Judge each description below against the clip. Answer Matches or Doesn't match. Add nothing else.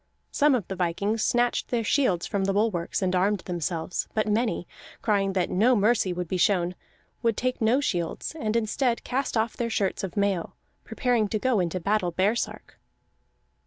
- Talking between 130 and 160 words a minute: Doesn't match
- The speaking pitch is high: Matches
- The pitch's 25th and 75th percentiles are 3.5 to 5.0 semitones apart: Matches